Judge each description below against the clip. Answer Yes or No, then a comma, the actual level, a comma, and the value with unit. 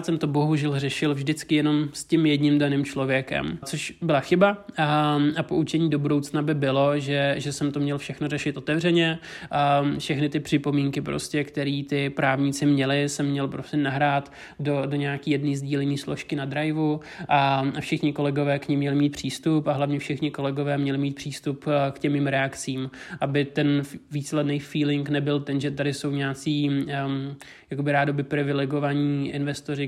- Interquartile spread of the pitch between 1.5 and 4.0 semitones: No, narrow, 1.1 semitones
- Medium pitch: Yes, medium, 145 Hz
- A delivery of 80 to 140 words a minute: No, average, 165 wpm